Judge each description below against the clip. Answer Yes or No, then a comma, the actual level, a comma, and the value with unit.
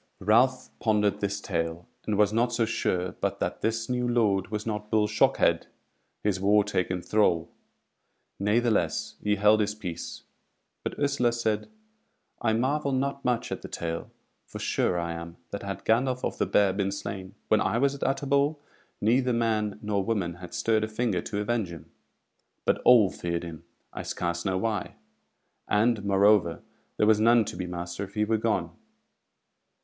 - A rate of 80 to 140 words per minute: No, average, 170 wpm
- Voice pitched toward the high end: No, low, 105 Hz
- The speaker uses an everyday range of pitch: Yes, average, 3.5 semitones